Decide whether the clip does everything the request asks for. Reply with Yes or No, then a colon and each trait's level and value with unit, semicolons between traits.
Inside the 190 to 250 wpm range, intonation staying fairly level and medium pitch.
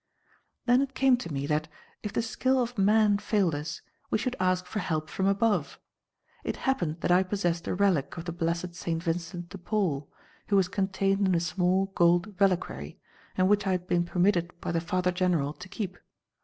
No: average, 195 wpm; average, 3.0 semitones; medium, 180 Hz